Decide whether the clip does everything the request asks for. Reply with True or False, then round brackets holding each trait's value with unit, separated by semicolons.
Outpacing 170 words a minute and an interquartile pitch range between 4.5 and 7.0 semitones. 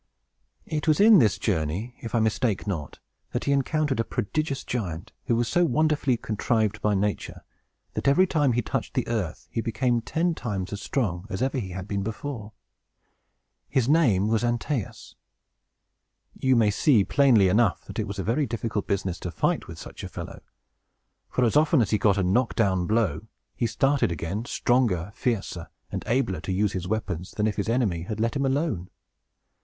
True (190 wpm; 5.0 semitones)